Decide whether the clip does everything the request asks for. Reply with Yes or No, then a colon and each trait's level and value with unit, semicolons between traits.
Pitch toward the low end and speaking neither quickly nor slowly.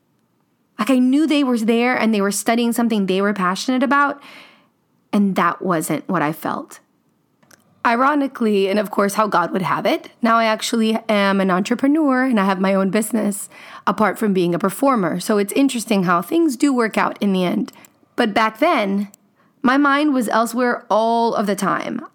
No: high, 220 Hz; average, 185 wpm